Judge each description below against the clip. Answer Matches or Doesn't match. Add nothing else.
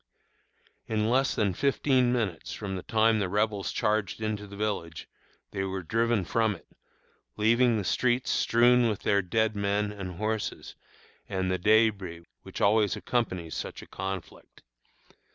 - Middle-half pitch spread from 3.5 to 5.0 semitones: Doesn't match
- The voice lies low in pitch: Matches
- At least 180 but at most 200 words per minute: Doesn't match